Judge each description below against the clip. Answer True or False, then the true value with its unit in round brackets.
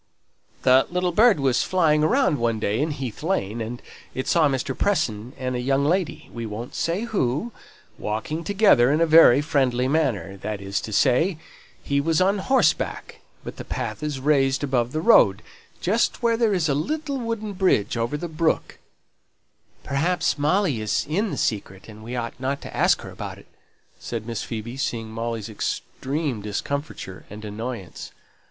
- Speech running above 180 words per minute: False (175 wpm)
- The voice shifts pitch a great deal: True (6.3 semitones)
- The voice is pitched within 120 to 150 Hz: True (135 Hz)